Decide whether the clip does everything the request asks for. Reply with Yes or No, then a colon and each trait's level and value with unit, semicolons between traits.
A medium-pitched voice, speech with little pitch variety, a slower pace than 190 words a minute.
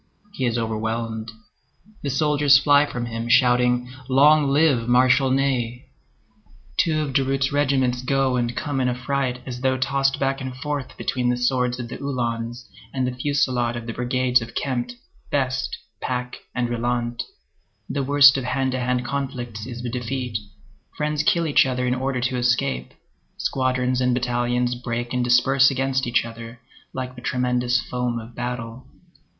No: low, 125 Hz; narrow, 1.8 semitones; average, 160 wpm